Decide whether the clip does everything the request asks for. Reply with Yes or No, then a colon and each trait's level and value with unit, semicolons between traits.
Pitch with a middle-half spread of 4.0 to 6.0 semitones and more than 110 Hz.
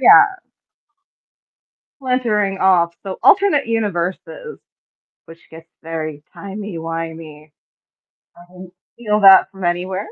Yes: average, 4.3 semitones; high, 190 Hz